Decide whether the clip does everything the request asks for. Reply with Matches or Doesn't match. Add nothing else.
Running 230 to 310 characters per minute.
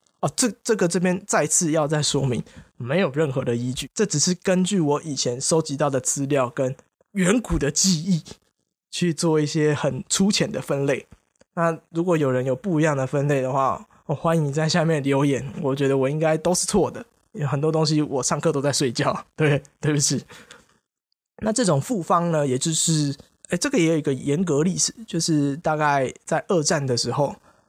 Matches